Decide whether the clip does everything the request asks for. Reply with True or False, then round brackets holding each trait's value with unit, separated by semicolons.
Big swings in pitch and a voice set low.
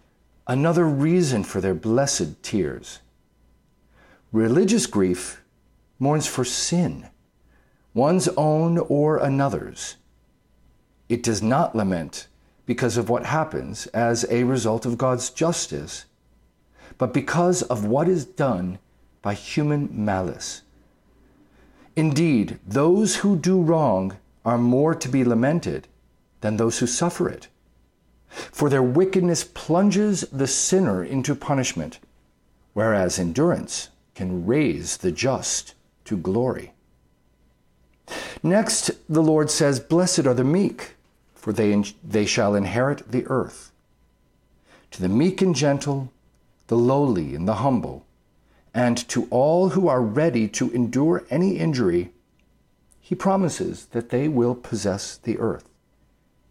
True (6.8 semitones; 130 Hz)